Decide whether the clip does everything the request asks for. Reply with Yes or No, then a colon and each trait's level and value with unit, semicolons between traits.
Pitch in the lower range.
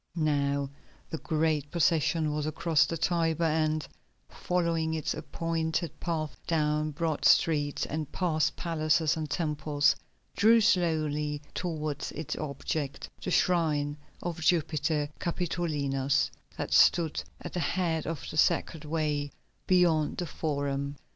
No: medium, 155 Hz